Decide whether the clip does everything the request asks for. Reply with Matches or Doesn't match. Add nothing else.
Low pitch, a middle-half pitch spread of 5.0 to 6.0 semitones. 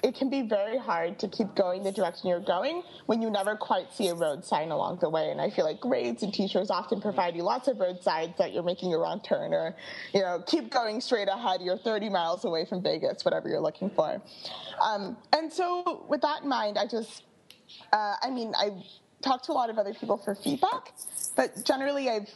Doesn't match